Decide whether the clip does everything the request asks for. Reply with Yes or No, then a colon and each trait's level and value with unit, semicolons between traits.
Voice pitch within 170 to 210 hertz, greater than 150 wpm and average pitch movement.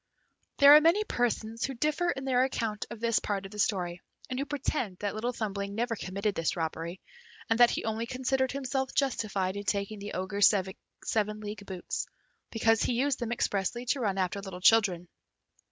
No: high, 220 Hz; average, 185 wpm; average, 4.2 semitones